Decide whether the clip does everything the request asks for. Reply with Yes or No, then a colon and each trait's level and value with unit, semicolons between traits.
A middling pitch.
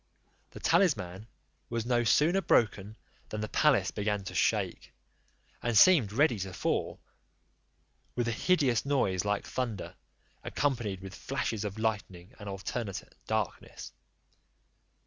No: low, 110 Hz